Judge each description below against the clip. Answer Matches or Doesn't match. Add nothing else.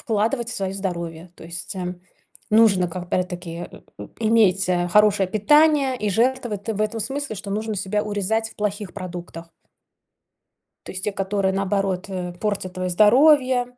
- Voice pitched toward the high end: Matches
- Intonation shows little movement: Doesn't match